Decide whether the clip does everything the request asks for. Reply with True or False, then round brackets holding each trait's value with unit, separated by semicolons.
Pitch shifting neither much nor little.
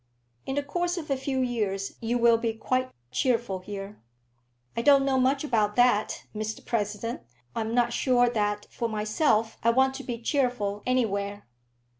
True (3.5 semitones)